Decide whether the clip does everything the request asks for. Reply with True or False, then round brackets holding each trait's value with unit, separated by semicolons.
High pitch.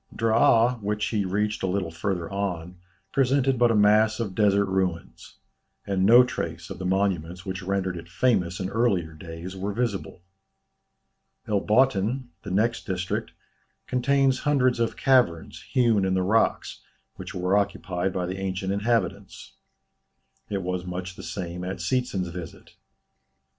False (100 Hz)